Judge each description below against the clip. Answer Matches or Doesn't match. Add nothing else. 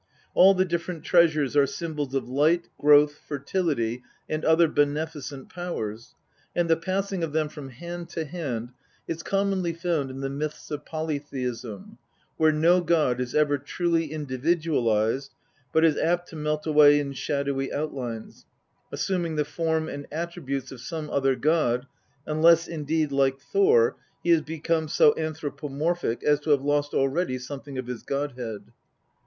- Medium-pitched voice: Matches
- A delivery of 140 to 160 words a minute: Matches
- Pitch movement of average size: Matches